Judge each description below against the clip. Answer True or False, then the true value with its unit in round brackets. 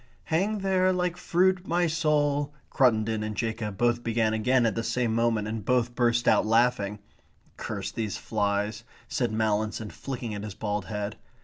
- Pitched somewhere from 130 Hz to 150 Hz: False (115 Hz)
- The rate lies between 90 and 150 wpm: False (165 wpm)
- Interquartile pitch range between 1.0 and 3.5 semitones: False (4.7 semitones)